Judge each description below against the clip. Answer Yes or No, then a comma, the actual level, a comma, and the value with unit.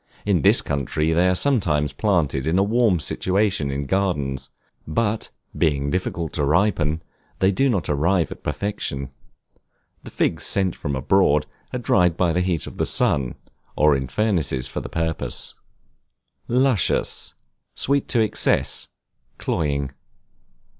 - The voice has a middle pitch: No, very low, 85 Hz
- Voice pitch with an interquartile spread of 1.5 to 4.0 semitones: No, wide, 5.5 semitones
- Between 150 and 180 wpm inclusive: No, average, 140 wpm